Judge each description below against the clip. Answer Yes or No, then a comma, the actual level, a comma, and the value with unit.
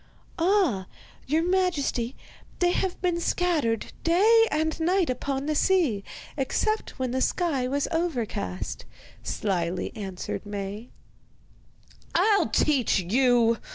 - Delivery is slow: Yes, slow, 110 wpm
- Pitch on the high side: Yes, very high, 280 Hz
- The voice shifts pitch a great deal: Yes, wide, 7.6 semitones